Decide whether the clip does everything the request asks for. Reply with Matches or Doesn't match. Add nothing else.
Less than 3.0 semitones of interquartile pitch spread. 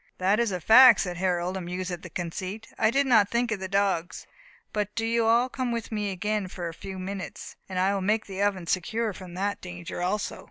Doesn't match